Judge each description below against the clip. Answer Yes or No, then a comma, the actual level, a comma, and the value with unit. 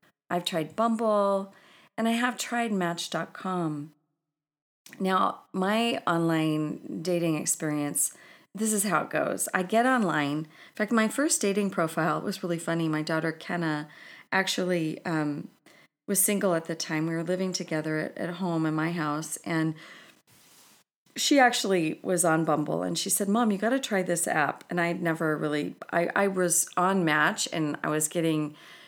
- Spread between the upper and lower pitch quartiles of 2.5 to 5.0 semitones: Yes, average, 4.0 semitones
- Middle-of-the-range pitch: Yes, medium, 170 Hz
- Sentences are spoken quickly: No, average, 160 wpm